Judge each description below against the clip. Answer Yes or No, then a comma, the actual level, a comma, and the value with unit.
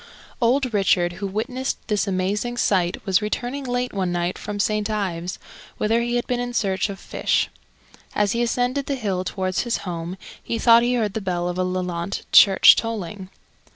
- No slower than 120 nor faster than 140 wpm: No, average, 180 wpm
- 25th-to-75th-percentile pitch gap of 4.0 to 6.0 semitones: Yes, average, 4.4 semitones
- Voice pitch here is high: Yes, high, 205 Hz